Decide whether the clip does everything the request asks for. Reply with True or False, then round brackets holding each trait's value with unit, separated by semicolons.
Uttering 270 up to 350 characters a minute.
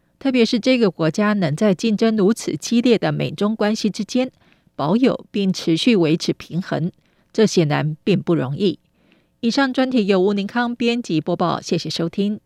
False (260 characters per minute)